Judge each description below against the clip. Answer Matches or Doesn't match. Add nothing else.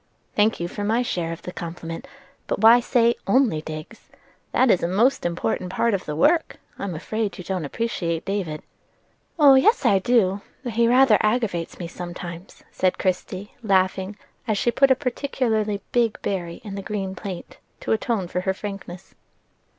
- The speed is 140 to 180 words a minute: Matches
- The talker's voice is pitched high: Matches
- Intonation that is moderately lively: Matches